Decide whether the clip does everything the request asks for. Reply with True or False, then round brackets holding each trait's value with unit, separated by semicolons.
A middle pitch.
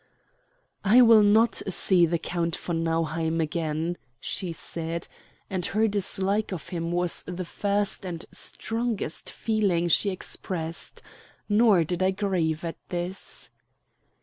True (180 Hz)